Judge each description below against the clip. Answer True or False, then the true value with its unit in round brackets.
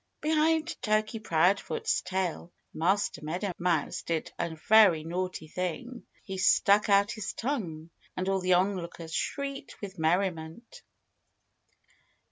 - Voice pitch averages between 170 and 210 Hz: True (190 Hz)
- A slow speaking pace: True (115 wpm)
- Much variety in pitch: False (4.3 semitones)